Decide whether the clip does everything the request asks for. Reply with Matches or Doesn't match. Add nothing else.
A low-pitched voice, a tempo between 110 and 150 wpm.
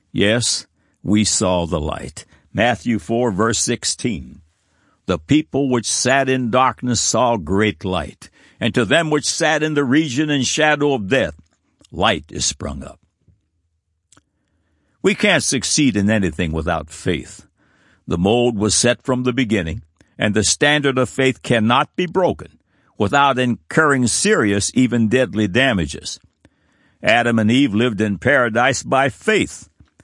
Matches